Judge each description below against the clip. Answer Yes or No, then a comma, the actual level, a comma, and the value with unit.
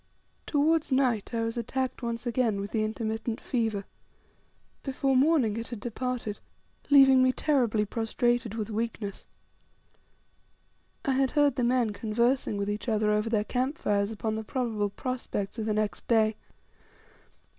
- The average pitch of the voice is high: Yes, high, 230 Hz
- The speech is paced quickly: No, average, 145 wpm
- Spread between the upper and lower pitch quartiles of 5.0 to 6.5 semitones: No, average, 3.1 semitones